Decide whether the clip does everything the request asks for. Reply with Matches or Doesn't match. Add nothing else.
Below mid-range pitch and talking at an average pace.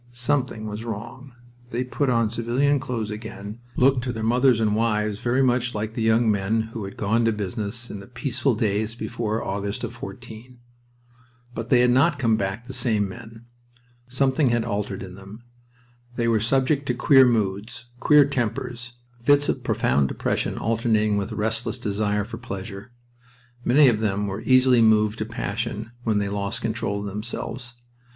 Matches